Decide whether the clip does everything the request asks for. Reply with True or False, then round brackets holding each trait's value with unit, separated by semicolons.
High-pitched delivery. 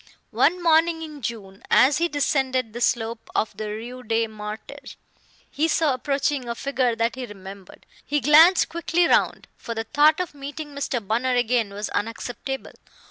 True (255 Hz)